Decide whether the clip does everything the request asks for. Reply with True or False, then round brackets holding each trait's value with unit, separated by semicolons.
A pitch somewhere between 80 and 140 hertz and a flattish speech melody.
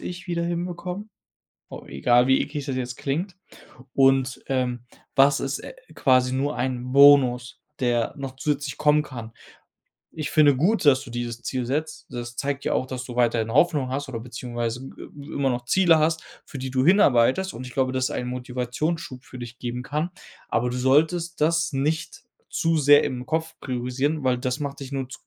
False (135 Hz; 3.3 semitones)